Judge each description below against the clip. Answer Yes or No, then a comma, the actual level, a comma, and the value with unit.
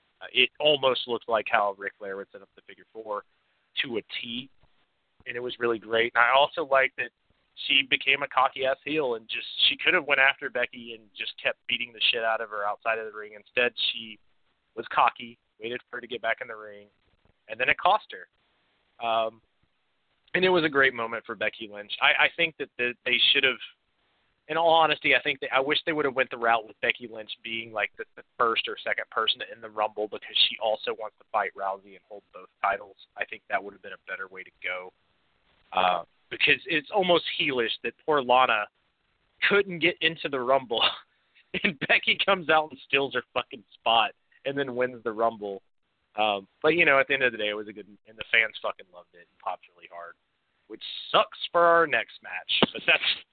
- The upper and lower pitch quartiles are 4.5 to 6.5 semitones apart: Yes, average, 5.1 semitones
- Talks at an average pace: No, fast, 225 wpm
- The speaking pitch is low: Yes, low, 115 Hz